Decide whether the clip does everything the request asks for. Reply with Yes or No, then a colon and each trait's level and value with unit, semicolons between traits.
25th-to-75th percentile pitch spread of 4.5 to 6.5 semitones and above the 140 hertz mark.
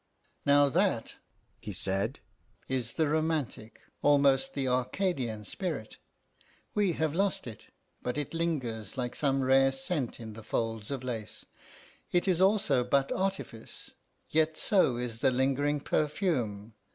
No: average, 5.1 semitones; low, 135 Hz